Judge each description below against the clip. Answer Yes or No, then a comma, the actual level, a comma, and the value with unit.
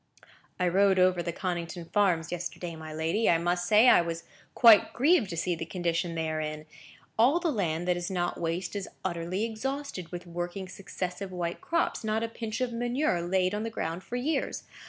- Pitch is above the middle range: No, medium, 180 Hz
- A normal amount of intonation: Yes, average, 4.4 semitones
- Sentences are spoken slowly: No, average, 200 wpm